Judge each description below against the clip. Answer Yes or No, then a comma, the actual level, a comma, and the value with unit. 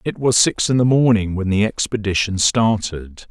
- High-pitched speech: No, low, 105 Hz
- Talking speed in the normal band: Yes, average, 180 wpm